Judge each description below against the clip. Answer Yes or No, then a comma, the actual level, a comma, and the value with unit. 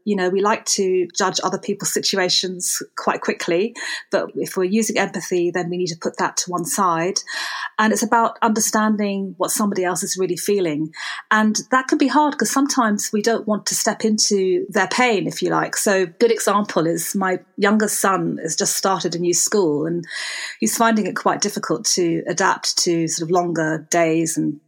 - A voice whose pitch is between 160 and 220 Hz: Yes, high, 190 Hz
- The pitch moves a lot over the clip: No, average, 3.4 semitones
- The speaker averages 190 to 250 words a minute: Yes, average, 195 wpm